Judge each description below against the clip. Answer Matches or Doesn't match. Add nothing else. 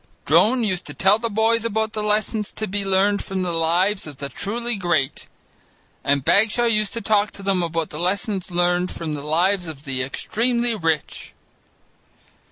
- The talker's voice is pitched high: Matches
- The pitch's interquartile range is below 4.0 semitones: Doesn't match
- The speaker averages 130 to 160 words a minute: Doesn't match